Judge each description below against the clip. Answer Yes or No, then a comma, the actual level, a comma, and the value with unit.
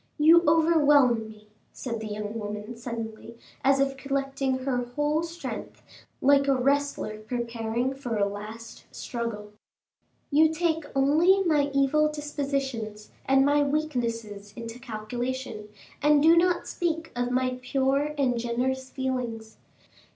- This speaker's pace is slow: Yes, slow, 130 wpm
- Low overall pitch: No, very high, 260 Hz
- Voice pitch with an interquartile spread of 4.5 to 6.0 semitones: No, average, 4.1 semitones